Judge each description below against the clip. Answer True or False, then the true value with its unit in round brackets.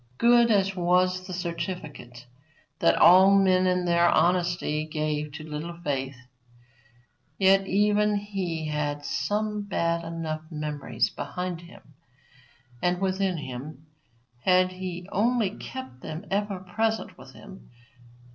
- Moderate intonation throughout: True (3.8 semitones)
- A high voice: False (180 Hz)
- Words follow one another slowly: True (120 wpm)